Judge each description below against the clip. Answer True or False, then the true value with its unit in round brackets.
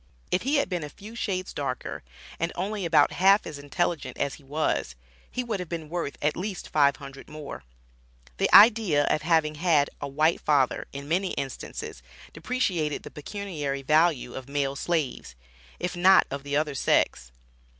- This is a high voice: False (155 Hz)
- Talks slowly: False (170 wpm)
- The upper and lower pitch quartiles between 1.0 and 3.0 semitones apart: False (4.3 semitones)